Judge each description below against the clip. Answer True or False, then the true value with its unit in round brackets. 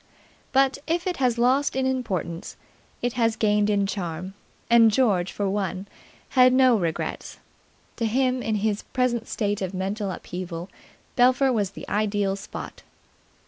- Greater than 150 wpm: False (145 wpm)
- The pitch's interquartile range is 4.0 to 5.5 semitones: True (4.5 semitones)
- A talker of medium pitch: False (215 Hz)